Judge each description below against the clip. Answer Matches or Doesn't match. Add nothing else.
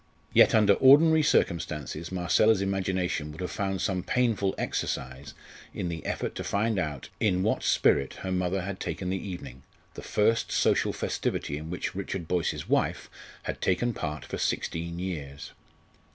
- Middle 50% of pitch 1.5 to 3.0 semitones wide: Doesn't match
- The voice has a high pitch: Doesn't match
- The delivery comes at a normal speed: Matches